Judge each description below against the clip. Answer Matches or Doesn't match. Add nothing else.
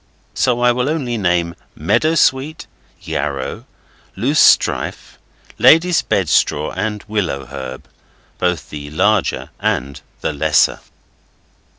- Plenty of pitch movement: Matches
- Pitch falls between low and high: Doesn't match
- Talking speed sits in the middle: Doesn't match